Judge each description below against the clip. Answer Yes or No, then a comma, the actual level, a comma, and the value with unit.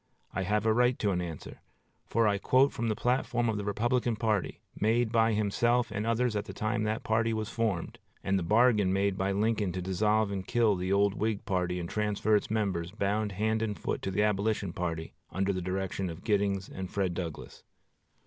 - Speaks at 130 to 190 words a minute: No, fast, 205 wpm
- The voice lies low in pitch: Yes, low, 105 Hz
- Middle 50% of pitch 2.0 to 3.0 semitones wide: Yes, narrow, 2.6 semitones